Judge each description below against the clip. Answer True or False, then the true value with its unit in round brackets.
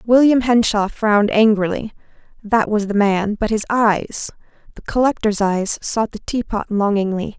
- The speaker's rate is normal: False (120 wpm)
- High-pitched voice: True (215 Hz)